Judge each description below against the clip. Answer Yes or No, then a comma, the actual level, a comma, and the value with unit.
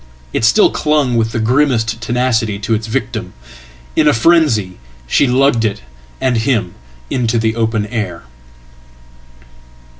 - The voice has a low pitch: Yes, low, 115 Hz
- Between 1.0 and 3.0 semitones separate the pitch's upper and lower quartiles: Yes, average, 2.7 semitones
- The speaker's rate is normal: No, slow, 125 wpm